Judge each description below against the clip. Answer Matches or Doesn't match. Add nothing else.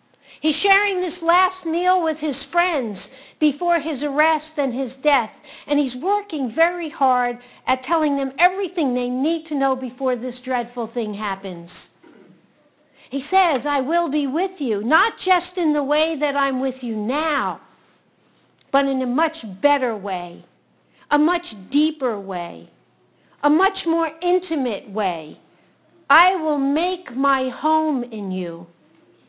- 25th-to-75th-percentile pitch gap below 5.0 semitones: Matches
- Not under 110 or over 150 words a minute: Matches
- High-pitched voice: Matches